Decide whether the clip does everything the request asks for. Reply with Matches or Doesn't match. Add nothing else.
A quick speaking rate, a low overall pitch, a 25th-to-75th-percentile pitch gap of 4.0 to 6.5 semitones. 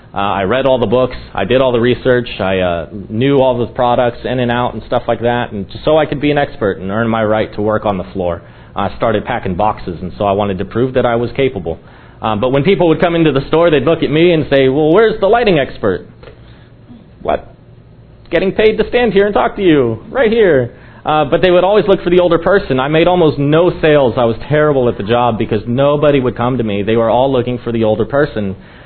Matches